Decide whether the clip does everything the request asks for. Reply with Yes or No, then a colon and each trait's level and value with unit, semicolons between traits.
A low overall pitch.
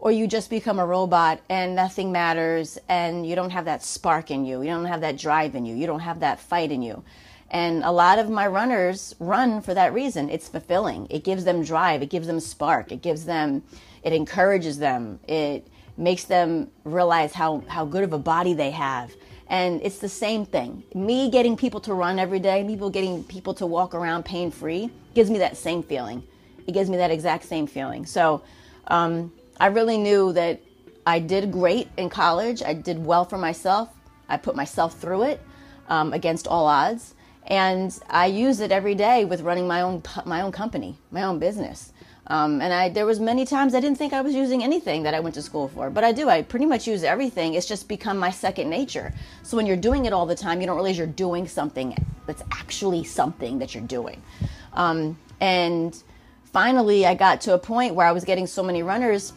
No: medium, 180 Hz